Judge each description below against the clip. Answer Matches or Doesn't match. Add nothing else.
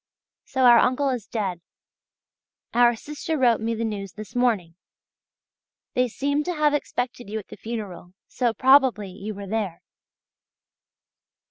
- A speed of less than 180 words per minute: Matches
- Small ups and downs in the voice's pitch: Doesn't match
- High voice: Matches